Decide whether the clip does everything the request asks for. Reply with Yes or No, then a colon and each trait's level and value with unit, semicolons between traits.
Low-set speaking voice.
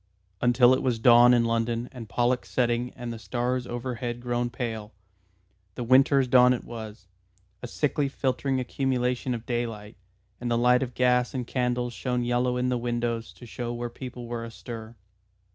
Yes: low, 120 Hz